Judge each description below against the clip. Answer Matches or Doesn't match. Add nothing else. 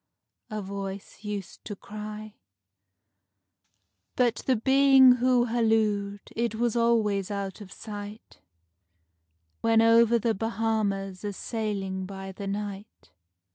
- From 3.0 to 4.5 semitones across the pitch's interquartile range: Doesn't match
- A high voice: Matches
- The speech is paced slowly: Matches